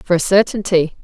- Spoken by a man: No, female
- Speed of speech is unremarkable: Yes, average, 175 wpm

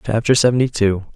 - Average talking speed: Yes, average, 155 wpm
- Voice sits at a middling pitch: No, low, 115 Hz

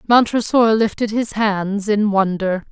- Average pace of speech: No, slow, 130 wpm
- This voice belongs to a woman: Yes, female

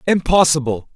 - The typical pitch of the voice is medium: Yes, medium, 150 Hz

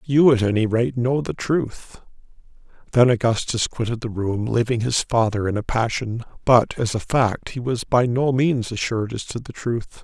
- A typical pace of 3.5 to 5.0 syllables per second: Yes, 4.7 syllables/s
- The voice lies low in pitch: Yes, low, 120 Hz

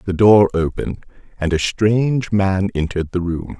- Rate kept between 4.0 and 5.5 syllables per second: Yes, 5.1 syllables/s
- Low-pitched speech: Yes, very low, 95 Hz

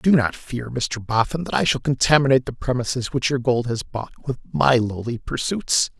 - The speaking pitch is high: No, low, 125 Hz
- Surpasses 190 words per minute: Yes, average, 200 wpm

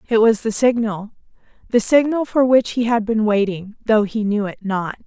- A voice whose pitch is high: Yes, high, 220 Hz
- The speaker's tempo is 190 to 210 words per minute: Yes, average, 200 wpm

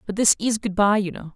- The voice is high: Yes, high, 200 Hz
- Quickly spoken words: Yes, fast, 310 wpm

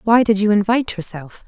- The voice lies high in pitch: Yes, high, 210 Hz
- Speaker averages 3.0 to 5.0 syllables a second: No, 5.8 syllables/s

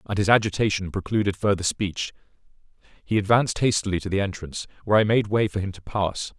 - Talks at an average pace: Yes, average, 190 wpm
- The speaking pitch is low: Yes, low, 100 Hz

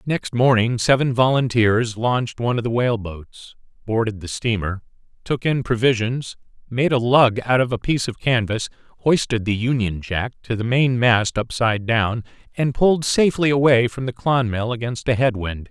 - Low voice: Yes, low, 120 Hz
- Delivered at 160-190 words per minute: Yes, average, 170 wpm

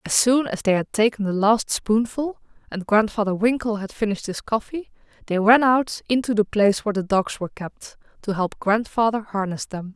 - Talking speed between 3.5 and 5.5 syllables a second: Yes, 5.3 syllables/s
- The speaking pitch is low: No, high, 215 Hz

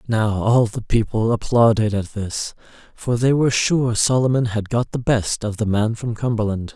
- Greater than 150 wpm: Yes, average, 185 wpm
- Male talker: Yes, male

